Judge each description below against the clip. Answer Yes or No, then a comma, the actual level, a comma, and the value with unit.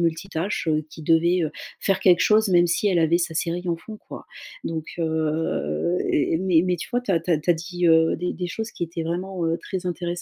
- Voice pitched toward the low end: No, medium, 170 Hz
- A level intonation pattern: Yes, narrow, 2.0 semitones